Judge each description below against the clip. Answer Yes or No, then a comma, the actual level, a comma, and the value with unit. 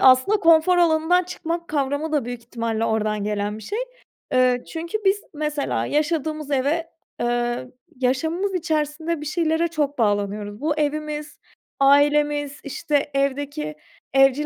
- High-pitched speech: Yes, very high, 290 Hz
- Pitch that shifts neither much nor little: Yes, average, 4.1 semitones